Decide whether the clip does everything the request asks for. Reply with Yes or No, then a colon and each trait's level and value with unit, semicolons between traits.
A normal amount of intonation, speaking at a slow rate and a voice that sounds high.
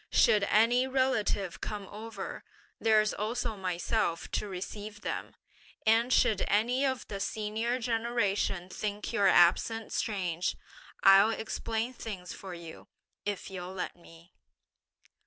Yes: average, 3.0 semitones; slow, 120 wpm; high, 210 Hz